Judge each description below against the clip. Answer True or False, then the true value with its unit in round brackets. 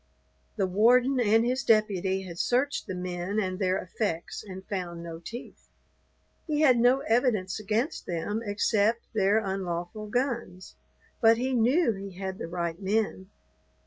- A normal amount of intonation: True (4.1 semitones)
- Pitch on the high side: True (205 Hz)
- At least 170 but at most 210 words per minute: False (145 wpm)